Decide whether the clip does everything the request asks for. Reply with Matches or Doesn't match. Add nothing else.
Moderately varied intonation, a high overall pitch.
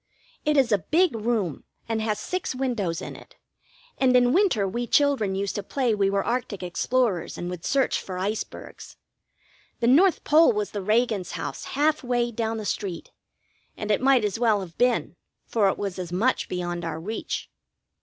Matches